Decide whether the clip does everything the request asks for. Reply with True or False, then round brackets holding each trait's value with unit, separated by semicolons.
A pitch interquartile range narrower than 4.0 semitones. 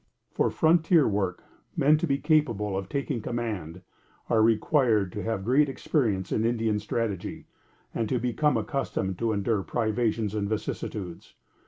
False (4.7 semitones)